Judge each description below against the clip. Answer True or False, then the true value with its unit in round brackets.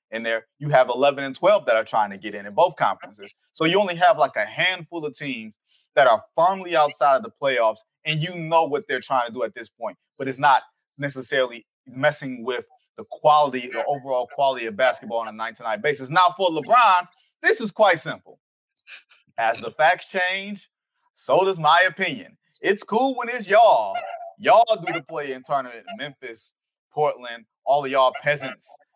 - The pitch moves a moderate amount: False (8.6 semitones)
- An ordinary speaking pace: True (195 wpm)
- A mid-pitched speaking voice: True (155 Hz)